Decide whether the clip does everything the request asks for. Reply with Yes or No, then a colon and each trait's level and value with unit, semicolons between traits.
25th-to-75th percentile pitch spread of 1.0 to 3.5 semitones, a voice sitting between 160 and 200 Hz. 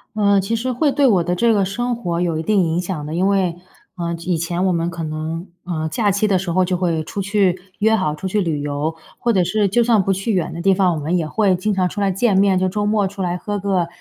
Yes: average, 3.2 semitones; medium, 185 Hz